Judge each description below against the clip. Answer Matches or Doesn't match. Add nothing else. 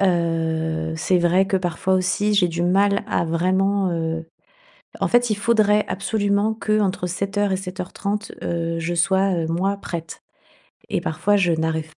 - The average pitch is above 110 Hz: Matches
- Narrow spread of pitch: Doesn't match